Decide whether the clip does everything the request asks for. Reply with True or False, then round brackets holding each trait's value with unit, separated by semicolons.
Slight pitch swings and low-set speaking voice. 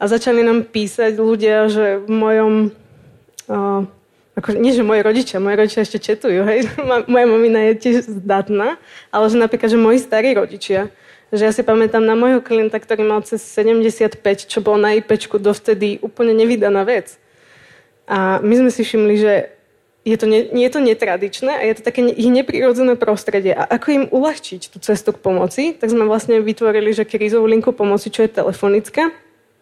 False (1.7 semitones; 220 Hz)